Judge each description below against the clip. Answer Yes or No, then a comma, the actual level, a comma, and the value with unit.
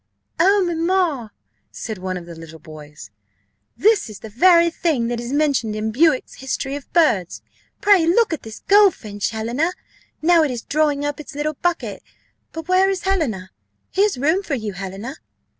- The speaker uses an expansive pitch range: Yes, wide, 7.7 semitones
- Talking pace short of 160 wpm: No, average, 170 wpm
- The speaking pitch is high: Yes, very high, 285 Hz